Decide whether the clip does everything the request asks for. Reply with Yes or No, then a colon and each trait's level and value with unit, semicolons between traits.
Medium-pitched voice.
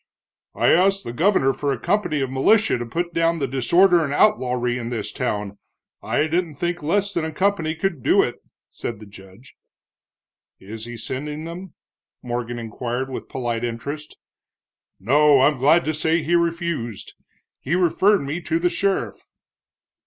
Yes: medium, 150 Hz